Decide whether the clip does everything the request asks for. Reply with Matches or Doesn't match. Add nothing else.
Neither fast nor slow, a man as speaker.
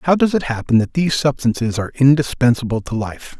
Matches